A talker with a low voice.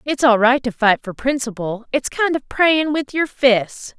No: very high, 255 Hz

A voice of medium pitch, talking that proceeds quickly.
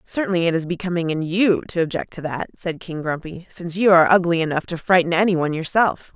Yes: medium, 170 Hz; fast, 215 wpm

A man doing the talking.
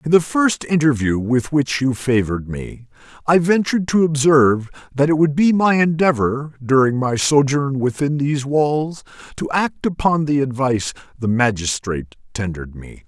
Yes: male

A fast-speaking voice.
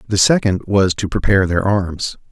No: average, 180 wpm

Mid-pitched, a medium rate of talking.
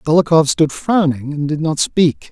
Yes: medium, 155 Hz; average, 180 wpm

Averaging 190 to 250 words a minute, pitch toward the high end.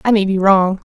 No: fast, 265 wpm; high, 195 Hz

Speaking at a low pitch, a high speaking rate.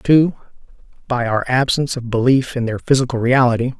No: low, 125 Hz; average, 160 wpm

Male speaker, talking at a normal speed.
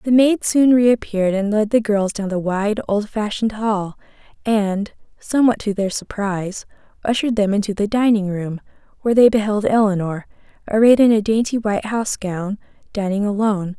No: female; average, 160 wpm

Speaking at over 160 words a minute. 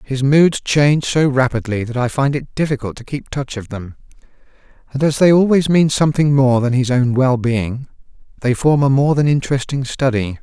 Yes: average, 190 wpm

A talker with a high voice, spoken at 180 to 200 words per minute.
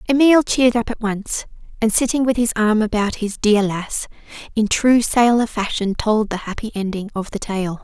Yes: high, 220 Hz; average, 190 wpm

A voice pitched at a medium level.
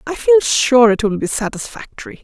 No: very high, 250 Hz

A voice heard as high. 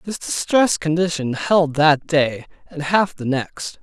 No: medium, 160 Hz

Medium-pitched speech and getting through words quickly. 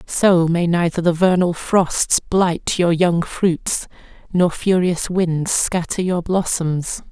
No: medium, 175 Hz; slow, 135 wpm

